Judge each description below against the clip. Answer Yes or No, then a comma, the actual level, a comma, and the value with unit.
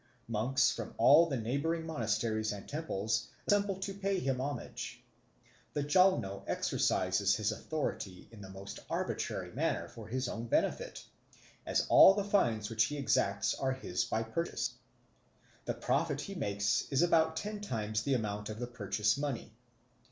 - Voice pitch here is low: Yes, low, 120 Hz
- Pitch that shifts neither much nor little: No, wide, 7.1 semitones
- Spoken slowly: No, average, 155 wpm